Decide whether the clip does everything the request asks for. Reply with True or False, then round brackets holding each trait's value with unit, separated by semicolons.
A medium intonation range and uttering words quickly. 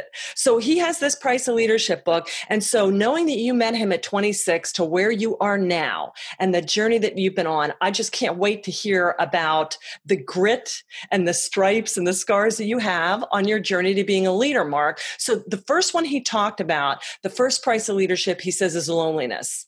True (4.0 semitones; 215 wpm)